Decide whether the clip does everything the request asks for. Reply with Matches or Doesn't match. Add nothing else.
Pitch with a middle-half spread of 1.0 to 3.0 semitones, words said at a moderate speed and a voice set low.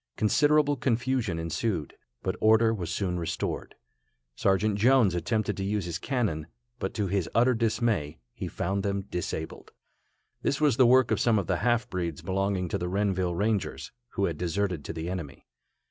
Doesn't match